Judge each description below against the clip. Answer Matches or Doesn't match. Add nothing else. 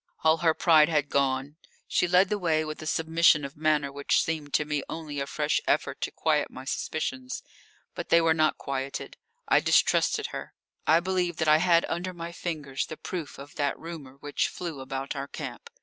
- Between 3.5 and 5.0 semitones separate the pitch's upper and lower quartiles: Doesn't match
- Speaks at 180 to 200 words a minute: Matches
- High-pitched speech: Doesn't match